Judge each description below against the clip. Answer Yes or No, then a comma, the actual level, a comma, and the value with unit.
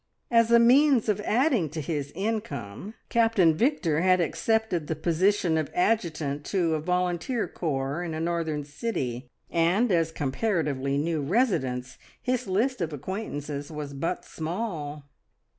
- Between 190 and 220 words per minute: No, average, 140 wpm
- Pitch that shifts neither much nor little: No, wide, 6.5 semitones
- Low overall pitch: No, medium, 170 Hz